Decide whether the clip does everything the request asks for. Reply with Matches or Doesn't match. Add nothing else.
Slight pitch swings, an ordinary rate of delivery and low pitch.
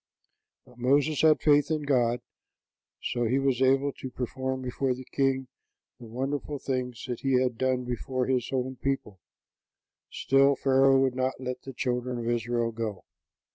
Matches